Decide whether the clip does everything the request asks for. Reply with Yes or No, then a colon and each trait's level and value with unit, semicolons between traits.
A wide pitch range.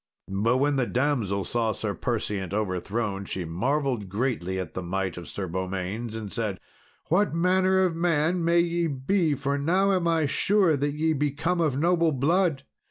Yes: wide, 8.6 semitones